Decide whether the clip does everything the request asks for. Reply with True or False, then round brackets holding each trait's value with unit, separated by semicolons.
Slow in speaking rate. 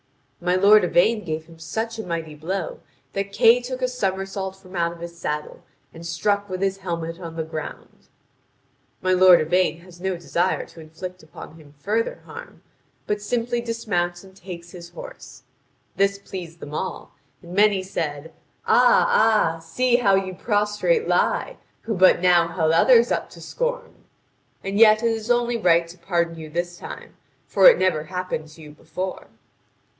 False (170 wpm)